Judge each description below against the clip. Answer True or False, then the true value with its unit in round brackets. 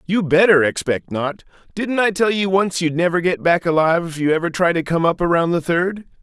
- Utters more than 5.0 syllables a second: True (5.5 syllables/s)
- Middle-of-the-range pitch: True (175 Hz)